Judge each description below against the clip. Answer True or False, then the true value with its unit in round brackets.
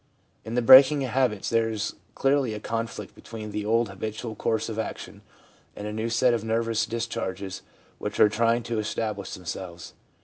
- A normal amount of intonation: False (1.7 semitones)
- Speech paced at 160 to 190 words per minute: True (175 wpm)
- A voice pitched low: True (115 Hz)